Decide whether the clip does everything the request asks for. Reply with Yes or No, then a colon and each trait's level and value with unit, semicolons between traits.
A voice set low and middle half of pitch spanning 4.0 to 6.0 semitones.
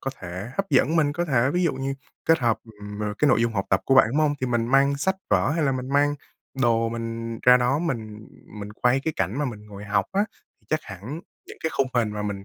Yes: low, 125 Hz; average, 5.2 semitones